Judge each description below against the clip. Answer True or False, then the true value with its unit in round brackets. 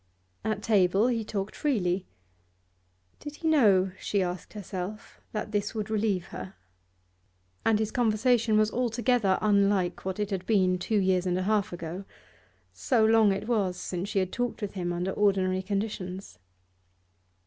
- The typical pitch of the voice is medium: False (205 Hz)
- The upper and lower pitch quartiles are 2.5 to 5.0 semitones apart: True (2.8 semitones)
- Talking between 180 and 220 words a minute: False (155 wpm)